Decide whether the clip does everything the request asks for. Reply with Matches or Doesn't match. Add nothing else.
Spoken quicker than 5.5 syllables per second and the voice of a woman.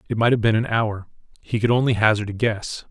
Doesn't match